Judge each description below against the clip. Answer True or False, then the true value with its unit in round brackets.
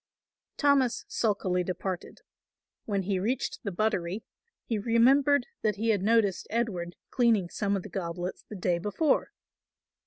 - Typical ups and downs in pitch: True (4.0 semitones)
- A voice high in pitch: True (205 Hz)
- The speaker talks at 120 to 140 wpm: True (135 wpm)